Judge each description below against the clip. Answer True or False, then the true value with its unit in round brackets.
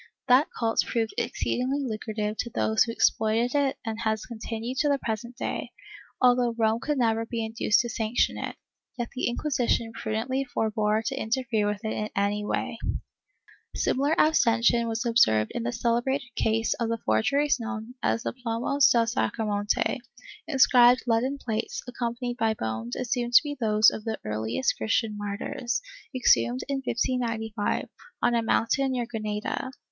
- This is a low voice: False (230 Hz)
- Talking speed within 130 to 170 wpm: True (160 wpm)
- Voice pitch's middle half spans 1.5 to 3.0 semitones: True (2.4 semitones)